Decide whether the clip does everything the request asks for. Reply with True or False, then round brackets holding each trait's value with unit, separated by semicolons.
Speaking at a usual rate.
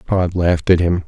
False (225 wpm)